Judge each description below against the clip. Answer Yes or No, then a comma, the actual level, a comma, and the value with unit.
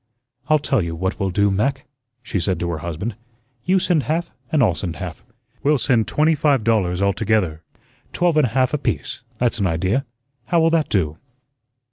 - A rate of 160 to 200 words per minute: Yes, average, 185 wpm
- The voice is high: No, low, 110 Hz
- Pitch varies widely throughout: Yes, wide, 7.8 semitones